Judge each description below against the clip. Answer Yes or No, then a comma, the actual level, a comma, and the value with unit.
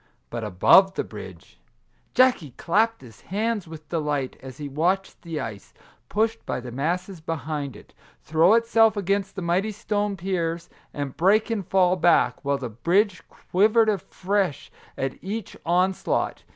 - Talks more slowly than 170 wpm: Yes, average, 150 wpm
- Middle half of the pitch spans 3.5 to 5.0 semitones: No, wide, 5.5 semitones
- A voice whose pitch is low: No, medium, 180 Hz